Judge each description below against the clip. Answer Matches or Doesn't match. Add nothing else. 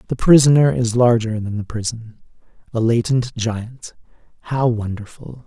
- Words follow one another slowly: Matches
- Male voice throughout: Matches